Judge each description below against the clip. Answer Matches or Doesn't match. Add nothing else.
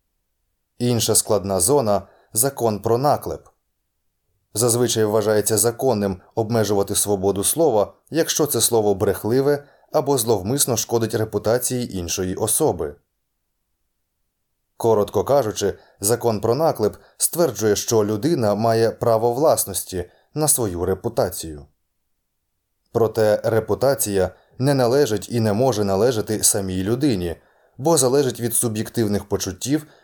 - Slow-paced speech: Matches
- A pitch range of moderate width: Matches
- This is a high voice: Doesn't match